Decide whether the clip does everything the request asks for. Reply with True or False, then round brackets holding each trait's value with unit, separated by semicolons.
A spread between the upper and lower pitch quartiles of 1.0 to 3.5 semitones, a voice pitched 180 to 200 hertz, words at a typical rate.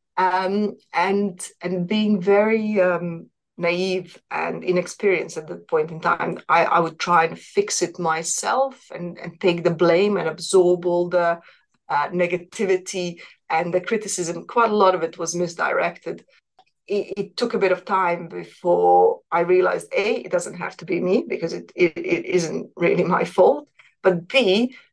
True (3.1 semitones; 185 Hz; 170 wpm)